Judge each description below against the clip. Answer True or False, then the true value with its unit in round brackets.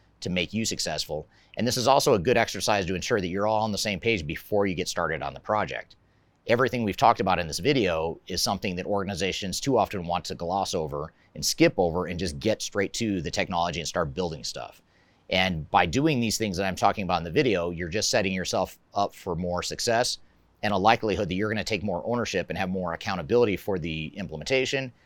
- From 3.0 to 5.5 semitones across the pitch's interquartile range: True (3.3 semitones)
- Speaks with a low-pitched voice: True (95 Hz)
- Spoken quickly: True (225 wpm)